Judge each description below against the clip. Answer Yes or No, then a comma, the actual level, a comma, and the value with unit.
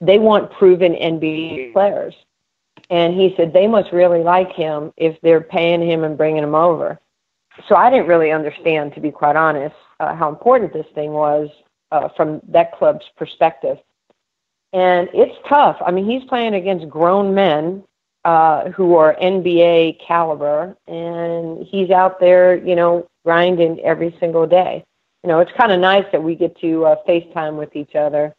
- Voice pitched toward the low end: No, medium, 170 Hz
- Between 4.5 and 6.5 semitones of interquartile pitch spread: No, narrow, 2.6 semitones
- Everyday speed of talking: Yes, average, 170 wpm